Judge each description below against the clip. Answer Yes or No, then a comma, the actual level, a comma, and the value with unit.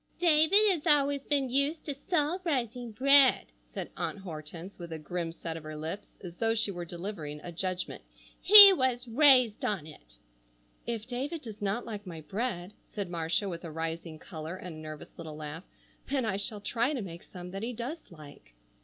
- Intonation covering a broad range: Yes, wide, 7.8 semitones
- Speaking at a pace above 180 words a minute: Yes, average, 190 wpm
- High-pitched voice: Yes, high, 205 Hz